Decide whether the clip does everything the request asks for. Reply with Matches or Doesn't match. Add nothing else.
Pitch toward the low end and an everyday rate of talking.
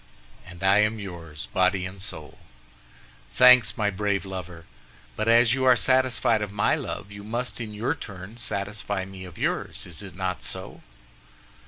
Matches